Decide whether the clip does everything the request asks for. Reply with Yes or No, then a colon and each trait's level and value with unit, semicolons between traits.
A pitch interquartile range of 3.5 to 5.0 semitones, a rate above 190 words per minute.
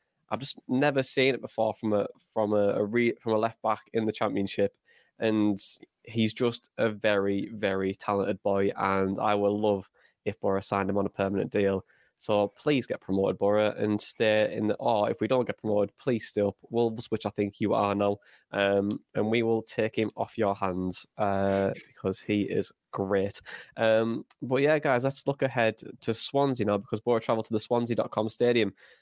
No: narrow, 2.5 semitones; average, 200 wpm